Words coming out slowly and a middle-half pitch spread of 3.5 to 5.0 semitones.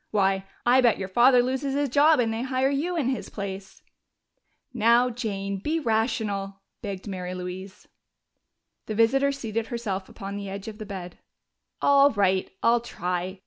No: average, 160 wpm; average, 4.6 semitones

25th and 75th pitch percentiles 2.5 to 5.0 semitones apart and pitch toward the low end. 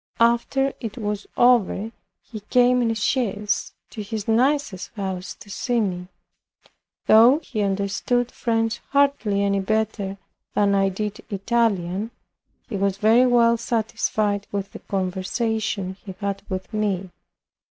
No: average, 2.9 semitones; high, 210 Hz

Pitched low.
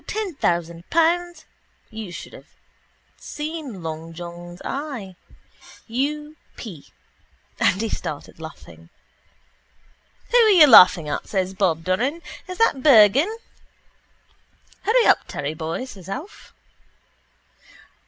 No: high, 220 Hz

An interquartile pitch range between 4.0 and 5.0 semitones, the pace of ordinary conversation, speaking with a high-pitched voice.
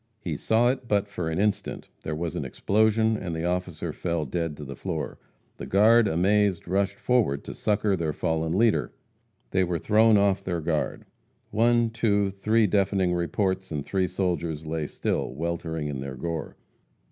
No: average, 4.3 semitones; average, 170 wpm; very low, 95 Hz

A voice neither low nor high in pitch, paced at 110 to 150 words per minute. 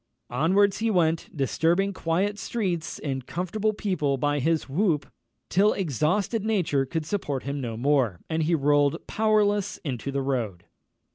Yes: medium, 160 Hz; average, 145 wpm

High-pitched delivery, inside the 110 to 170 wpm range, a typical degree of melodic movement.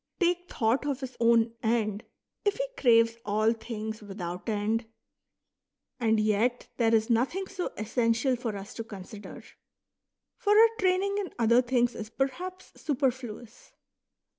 Yes: high, 230 Hz; average, 140 wpm; average, 3.6 semitones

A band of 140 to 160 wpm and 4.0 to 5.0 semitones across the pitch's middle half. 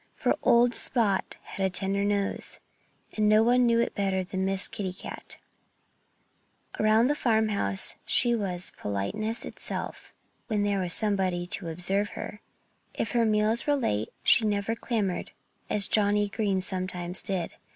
No: average, 150 wpm; average, 2.8 semitones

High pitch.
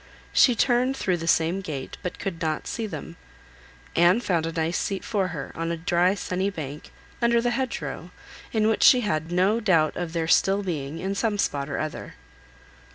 No: medium, 180 Hz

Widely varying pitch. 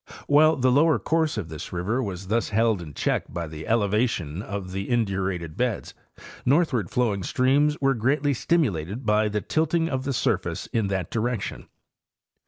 Yes: wide, 5.9 semitones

